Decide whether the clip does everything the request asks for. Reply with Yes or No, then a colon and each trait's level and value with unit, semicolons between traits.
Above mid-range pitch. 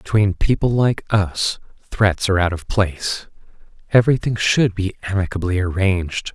No: low, 100 Hz